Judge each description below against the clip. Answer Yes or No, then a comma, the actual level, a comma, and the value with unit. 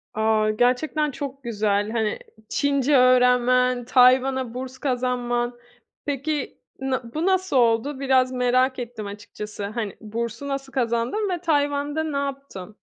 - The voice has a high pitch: Yes, very high, 255 Hz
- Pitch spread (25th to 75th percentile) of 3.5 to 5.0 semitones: No, average, 3.1 semitones